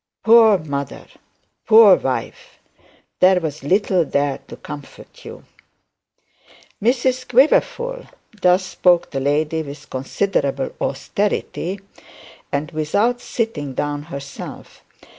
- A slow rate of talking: Yes, slow, 100 wpm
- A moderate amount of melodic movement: No, wide, 7.2 semitones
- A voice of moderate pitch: Yes, medium, 170 Hz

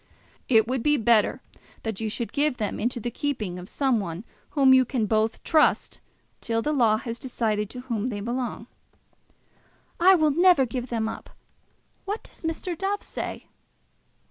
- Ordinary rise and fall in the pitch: Yes, average, 4.5 semitones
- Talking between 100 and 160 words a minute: No, average, 170 wpm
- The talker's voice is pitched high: Yes, high, 240 Hz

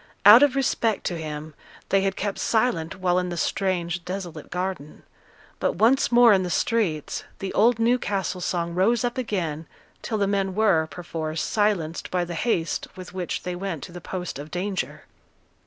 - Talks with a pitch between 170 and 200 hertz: Yes, medium, 185 Hz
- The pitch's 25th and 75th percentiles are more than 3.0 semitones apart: Yes, average, 3.7 semitones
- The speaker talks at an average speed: Yes, average, 175 wpm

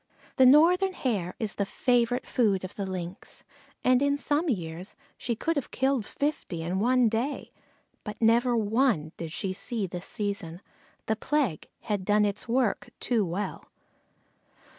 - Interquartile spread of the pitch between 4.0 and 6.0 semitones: Yes, average, 5.2 semitones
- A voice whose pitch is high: Yes, high, 220 Hz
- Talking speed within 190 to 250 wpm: No, average, 155 wpm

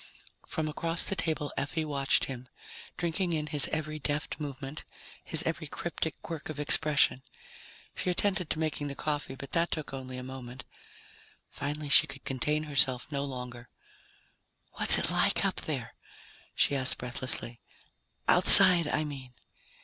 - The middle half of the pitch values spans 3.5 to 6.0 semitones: No, average, 2.8 semitones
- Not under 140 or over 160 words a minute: Yes, average, 150 wpm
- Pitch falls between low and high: Yes, medium, 145 Hz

